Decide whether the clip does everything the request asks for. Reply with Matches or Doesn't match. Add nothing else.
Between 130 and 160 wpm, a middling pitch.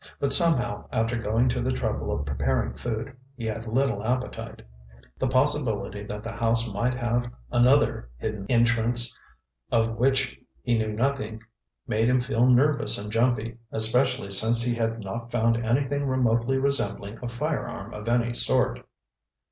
Doesn't match